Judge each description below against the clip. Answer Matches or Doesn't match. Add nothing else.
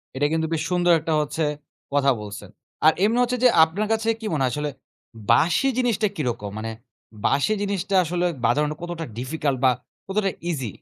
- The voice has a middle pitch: Matches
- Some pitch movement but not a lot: Doesn't match